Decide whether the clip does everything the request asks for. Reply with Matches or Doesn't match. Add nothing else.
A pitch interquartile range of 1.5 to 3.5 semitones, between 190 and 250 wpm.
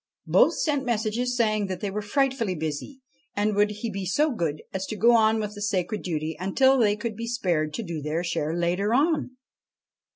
Doesn't match